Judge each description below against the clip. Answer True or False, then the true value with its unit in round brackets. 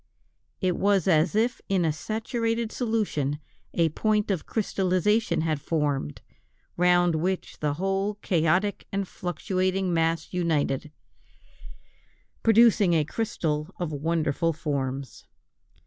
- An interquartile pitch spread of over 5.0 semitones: False (4.6 semitones)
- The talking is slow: True (110 wpm)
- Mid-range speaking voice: True (175 Hz)